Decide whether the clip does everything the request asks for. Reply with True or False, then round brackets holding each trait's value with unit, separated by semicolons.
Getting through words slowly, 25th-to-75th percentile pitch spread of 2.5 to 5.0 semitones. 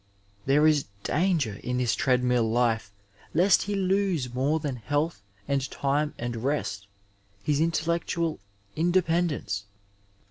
False (130 wpm; 5.4 semitones)